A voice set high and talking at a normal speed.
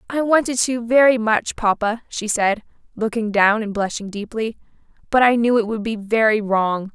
Yes: high, 220 Hz; average, 180 wpm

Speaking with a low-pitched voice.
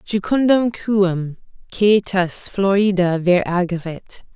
No: high, 190 Hz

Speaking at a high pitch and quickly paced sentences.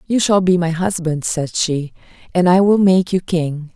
No: medium, 175 Hz; fast, 210 wpm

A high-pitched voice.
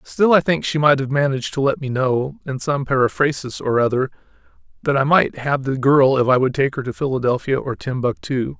No: low, 135 Hz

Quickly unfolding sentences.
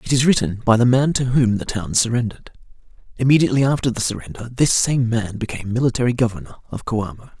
No: average, 185 wpm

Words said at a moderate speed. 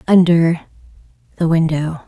No: slow, 85 wpm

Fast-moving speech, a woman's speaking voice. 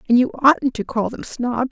Yes: fast, 245 wpm; female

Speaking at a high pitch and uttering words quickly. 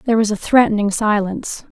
No: high, 215 Hz; average, 170 wpm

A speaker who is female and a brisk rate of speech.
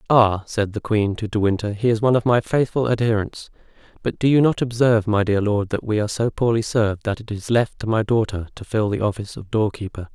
No: male; fast, 245 wpm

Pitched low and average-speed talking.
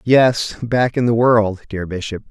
Yes: low, 115 Hz; average, 180 wpm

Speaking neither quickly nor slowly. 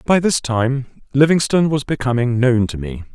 Yes: average, 170 wpm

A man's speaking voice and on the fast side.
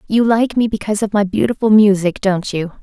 No: female; fast, 210 wpm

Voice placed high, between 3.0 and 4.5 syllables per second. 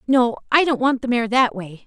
No: high, 240 Hz; 5.1 syllables/s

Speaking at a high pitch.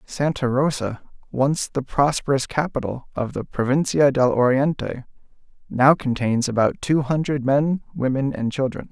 No: low, 135 Hz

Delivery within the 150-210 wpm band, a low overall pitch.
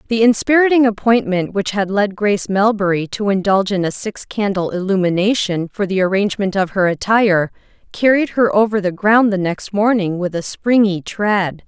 No: average, 170 wpm; high, 200 Hz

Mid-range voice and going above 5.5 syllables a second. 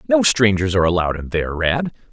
No: low, 100 Hz; 6.6 syllables/s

